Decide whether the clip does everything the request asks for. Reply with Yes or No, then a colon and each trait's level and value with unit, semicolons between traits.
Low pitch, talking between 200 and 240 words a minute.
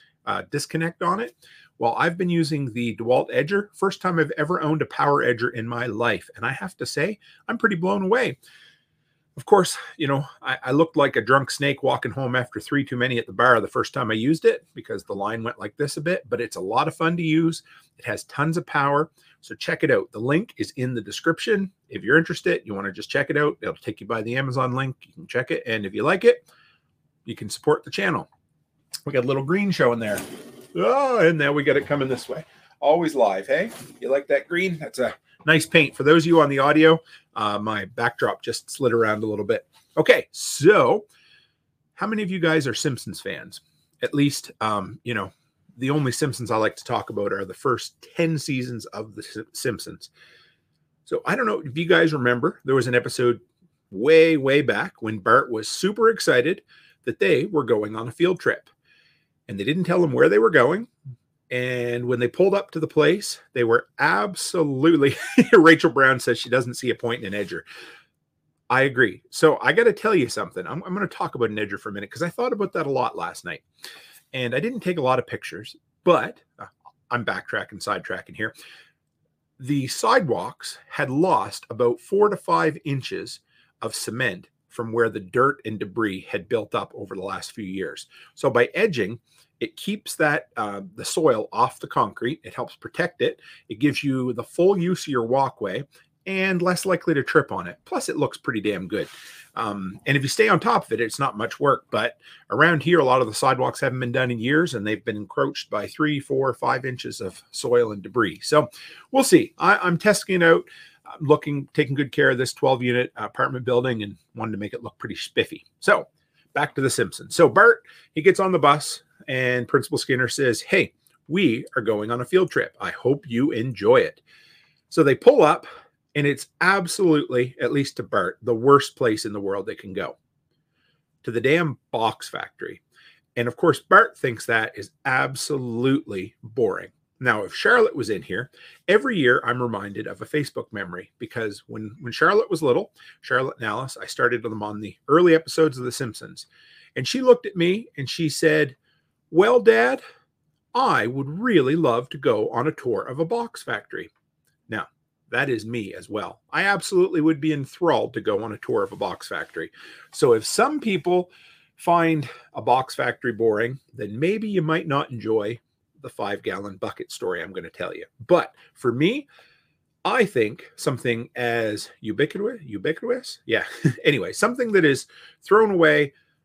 No: medium, 150 Hz; fast, 205 wpm